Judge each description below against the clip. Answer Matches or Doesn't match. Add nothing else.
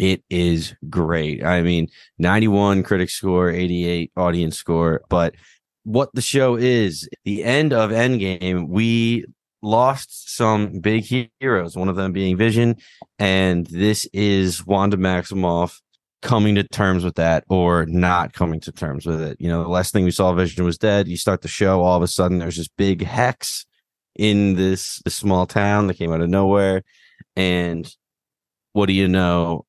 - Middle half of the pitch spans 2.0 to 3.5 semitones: Matches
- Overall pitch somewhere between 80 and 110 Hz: Matches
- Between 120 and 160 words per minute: Doesn't match